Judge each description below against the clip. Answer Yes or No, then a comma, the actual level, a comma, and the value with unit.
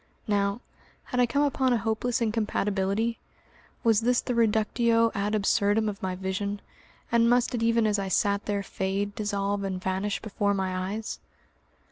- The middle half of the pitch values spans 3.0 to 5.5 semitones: No, narrow, 2.5 semitones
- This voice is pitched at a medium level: No, high, 210 Hz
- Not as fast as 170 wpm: Yes, average, 160 wpm